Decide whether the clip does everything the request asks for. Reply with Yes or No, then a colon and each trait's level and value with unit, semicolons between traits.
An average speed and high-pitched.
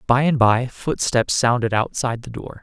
No: average, 185 wpm; low, 120 Hz